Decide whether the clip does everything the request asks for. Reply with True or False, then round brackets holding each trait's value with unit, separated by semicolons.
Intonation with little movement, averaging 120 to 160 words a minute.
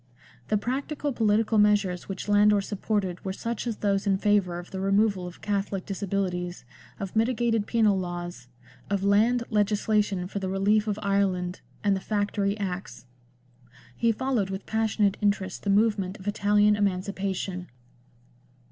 True (1.8 semitones; 145 wpm)